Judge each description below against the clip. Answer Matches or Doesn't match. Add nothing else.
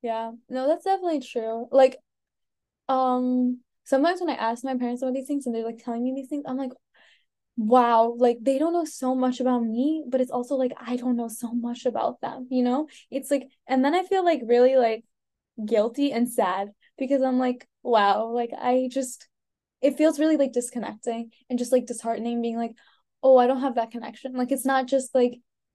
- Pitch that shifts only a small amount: Matches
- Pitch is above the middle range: Matches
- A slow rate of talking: Doesn't match